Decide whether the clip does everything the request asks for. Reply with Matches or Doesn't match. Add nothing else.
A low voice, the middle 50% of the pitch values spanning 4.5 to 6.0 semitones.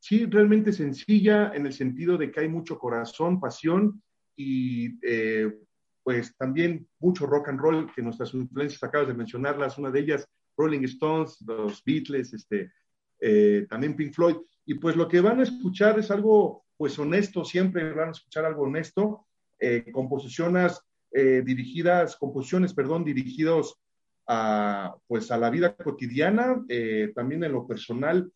Doesn't match